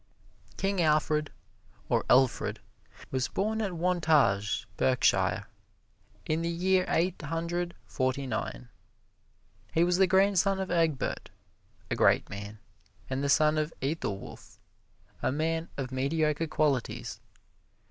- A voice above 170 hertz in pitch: No, medium, 155 Hz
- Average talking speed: No, slow, 115 wpm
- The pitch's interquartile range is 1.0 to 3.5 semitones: No, average, 4.7 semitones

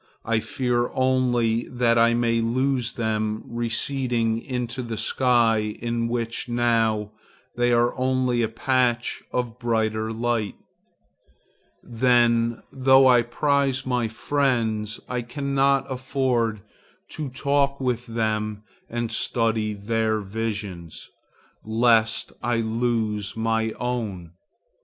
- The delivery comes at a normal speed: No, slow, 110 wpm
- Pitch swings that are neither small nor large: No, narrow, 2.0 semitones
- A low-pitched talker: Yes, low, 120 Hz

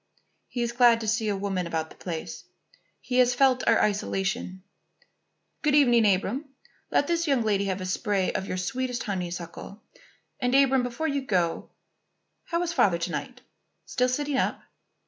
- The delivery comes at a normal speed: Yes, average, 165 wpm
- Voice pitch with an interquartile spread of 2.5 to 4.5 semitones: No, wide, 5.4 semitones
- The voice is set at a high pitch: Yes, high, 230 Hz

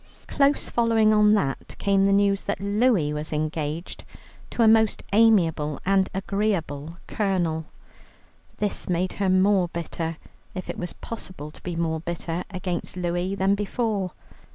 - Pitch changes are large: No, average, 3.7 semitones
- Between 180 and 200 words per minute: No, average, 145 wpm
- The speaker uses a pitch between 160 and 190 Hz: Yes, medium, 185 Hz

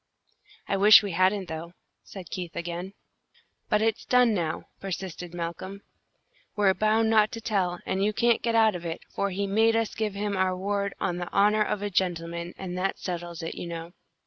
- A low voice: No, high, 195 Hz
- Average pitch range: Yes, average, 3.2 semitones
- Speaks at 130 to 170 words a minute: No, average, 195 wpm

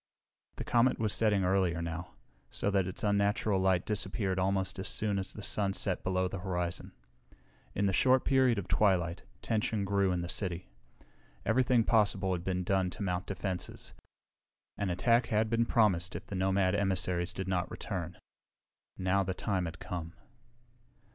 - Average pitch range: No, narrow, 2.2 semitones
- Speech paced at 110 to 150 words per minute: No, average, 165 wpm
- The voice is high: No, very low, 95 Hz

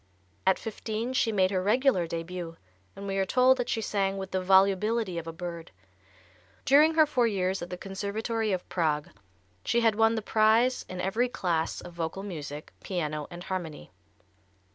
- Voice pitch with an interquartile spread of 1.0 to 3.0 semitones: No, average, 4.1 semitones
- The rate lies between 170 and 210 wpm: Yes, average, 175 wpm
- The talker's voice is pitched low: No, high, 195 Hz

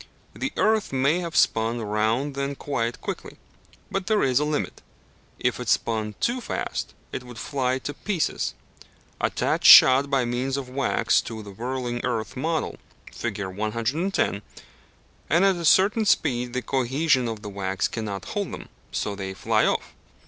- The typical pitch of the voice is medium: No, low, 130 Hz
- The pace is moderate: Yes, average, 160 wpm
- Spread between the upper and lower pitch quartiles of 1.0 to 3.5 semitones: No, average, 5.0 semitones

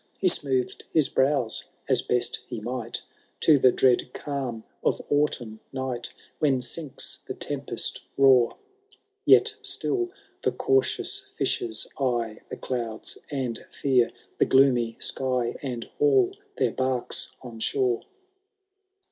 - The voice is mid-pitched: No, low, 130 Hz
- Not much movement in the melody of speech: No, average, 3.3 semitones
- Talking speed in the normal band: No, slow, 120 wpm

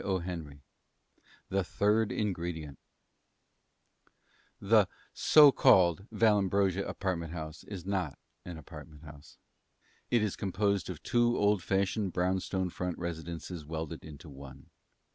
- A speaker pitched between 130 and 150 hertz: No, very low, 90 Hz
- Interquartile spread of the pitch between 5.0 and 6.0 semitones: No, average, 3.7 semitones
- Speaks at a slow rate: Yes, slow, 110 wpm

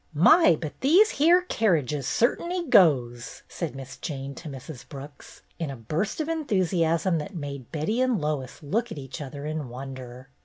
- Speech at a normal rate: Yes, average, 170 wpm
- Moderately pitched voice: Yes, medium, 155 Hz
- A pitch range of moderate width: No, wide, 7.8 semitones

